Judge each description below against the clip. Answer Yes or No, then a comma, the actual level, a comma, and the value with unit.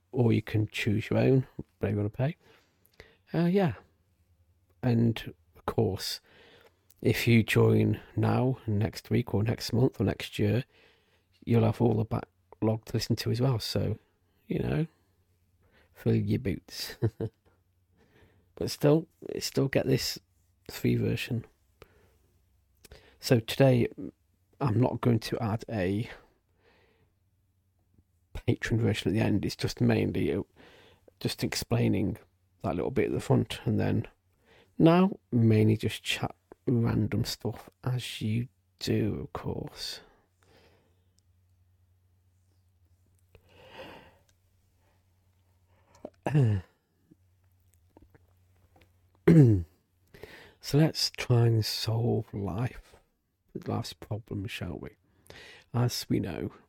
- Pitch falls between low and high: No, low, 100 Hz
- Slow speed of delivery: Yes, slow, 105 wpm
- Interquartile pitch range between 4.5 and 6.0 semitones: No, average, 4.1 semitones